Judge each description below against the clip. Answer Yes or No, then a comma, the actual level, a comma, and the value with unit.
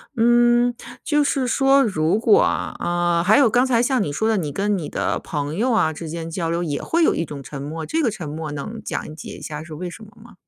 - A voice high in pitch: No, medium, 180 Hz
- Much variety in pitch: Yes, wide, 7.3 semitones